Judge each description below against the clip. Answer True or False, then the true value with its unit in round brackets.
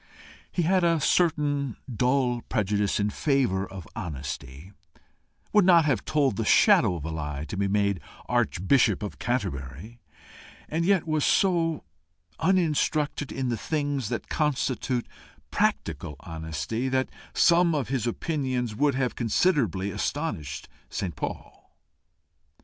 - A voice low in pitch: True (125 Hz)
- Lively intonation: True (7.6 semitones)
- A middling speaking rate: False (125 wpm)